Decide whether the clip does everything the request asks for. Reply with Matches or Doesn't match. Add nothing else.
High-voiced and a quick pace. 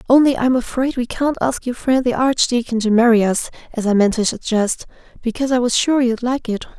Matches